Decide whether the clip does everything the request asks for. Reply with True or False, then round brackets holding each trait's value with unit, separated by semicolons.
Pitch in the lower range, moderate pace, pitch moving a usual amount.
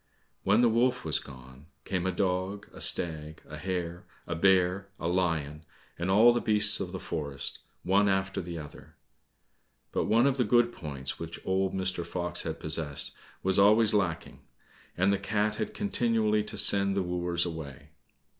True (95 Hz; 170 wpm; 3.8 semitones)